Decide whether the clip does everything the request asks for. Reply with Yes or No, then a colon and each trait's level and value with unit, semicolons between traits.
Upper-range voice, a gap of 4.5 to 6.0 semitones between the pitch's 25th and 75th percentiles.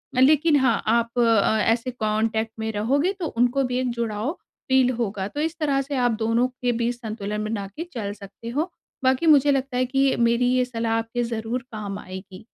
No: high, 235 Hz; average, 3.0 semitones